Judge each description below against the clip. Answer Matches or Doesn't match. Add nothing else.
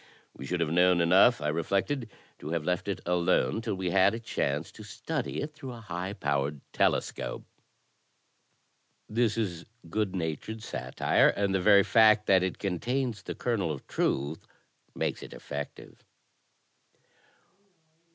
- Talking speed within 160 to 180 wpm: Doesn't match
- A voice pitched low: Matches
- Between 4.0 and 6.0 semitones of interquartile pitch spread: Matches